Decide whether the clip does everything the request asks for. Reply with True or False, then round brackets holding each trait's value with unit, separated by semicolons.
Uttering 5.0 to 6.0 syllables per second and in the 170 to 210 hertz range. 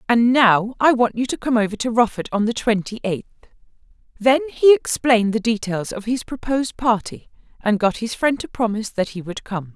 False (5.4 syllables/s; 225 Hz)